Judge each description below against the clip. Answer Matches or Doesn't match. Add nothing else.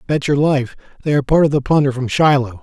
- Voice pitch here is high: Doesn't match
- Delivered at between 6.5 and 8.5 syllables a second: Matches